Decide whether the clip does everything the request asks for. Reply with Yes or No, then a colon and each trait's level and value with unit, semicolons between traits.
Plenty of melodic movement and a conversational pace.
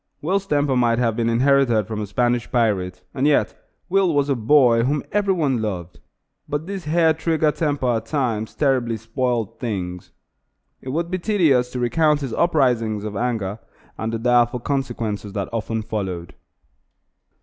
No: average, 4.9 semitones; average, 160 wpm